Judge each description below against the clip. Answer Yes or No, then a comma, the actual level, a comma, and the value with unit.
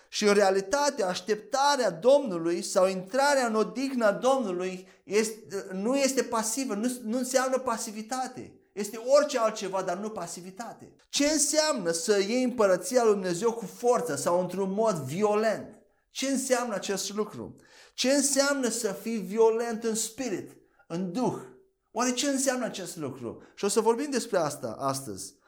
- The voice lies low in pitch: No, high, 225 Hz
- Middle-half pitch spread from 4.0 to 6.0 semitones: Yes, average, 5.1 semitones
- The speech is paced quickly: No, average, 145 wpm